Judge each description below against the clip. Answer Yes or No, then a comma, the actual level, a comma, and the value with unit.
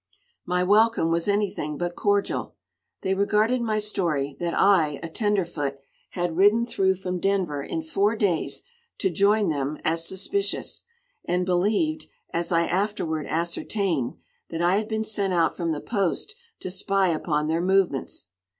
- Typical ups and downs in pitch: Yes, average, 3.7 semitones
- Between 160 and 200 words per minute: No, average, 150 wpm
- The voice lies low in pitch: No, medium, 185 Hz